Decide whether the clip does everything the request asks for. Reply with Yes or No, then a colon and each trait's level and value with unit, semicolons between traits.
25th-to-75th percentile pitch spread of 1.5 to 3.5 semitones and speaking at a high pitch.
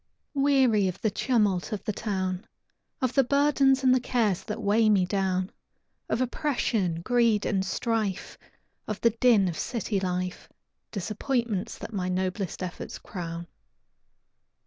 No: average, 4.4 semitones; high, 210 Hz